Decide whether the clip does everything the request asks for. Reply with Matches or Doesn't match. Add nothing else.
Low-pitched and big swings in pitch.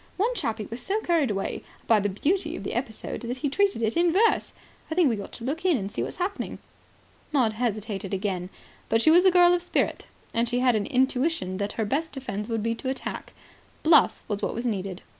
Doesn't match